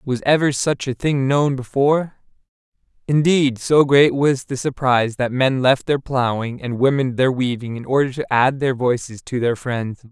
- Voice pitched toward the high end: No, low, 130 Hz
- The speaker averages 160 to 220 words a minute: Yes, average, 185 wpm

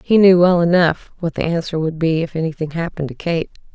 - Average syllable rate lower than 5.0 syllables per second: No, 6.0 syllables/s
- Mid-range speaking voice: Yes, medium, 165 Hz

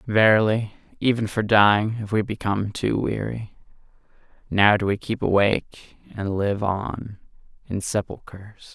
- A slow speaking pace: Yes, slow, 125 wpm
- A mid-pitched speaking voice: No, low, 105 Hz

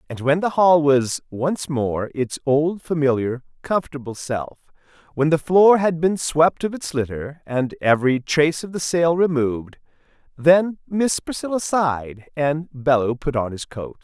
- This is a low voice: No, medium, 150 Hz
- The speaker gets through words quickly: No, average, 160 wpm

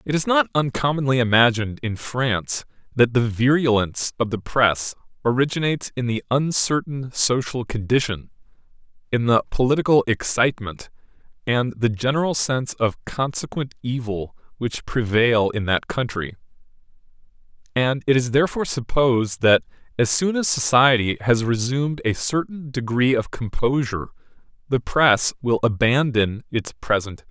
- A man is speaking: Yes, male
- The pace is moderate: No, slow, 130 wpm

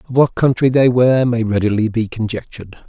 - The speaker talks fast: No, average, 190 wpm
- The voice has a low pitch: Yes, low, 115 Hz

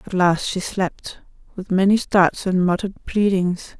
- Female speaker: Yes, female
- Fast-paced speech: No, average, 160 wpm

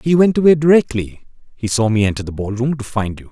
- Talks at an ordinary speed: No, fast, 255 wpm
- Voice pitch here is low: Yes, low, 125 Hz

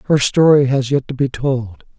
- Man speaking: Yes, male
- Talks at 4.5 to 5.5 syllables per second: Yes, 4.7 syllables/s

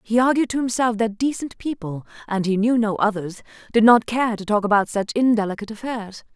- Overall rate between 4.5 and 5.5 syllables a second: No, 5.7 syllables/s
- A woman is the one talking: Yes, female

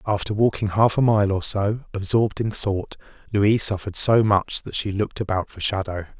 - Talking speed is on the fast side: No, average, 195 wpm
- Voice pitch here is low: Yes, low, 100 Hz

